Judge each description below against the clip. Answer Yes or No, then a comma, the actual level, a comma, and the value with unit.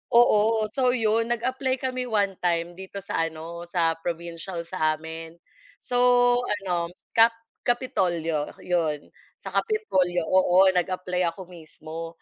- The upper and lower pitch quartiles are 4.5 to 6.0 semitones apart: Yes, average, 4.9 semitones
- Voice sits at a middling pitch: Yes, medium, 180 Hz